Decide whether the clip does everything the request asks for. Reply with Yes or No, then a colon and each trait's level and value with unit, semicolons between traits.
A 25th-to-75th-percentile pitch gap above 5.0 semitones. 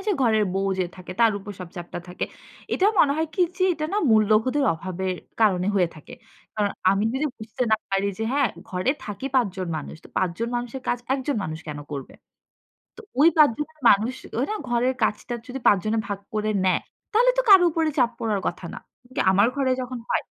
Yes: wide, 5.6 semitones